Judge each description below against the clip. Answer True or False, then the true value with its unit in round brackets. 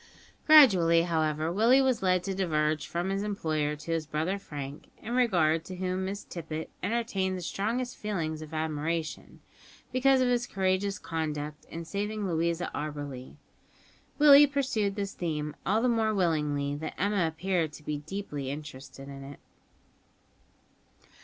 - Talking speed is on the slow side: False (145 wpm)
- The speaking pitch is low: False (170 Hz)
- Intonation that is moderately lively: True (4.9 semitones)